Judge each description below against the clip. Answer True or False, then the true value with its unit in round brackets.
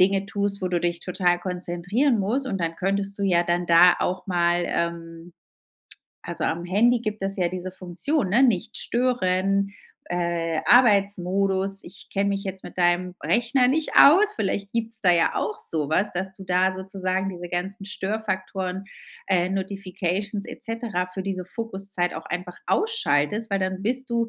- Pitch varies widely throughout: False (2.7 semitones)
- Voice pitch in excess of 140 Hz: True (190 Hz)